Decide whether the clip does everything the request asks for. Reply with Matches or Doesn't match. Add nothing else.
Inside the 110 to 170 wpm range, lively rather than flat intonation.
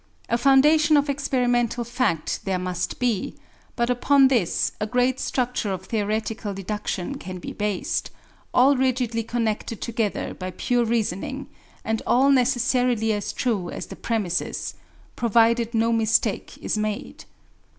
Doesn't match